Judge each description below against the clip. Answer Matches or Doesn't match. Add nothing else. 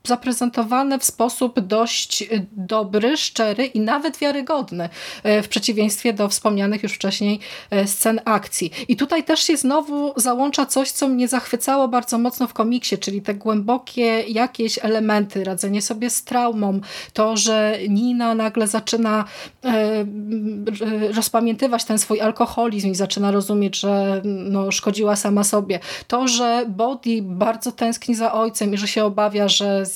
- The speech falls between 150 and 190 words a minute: Doesn't match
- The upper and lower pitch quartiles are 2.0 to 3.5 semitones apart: Matches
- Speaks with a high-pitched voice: Matches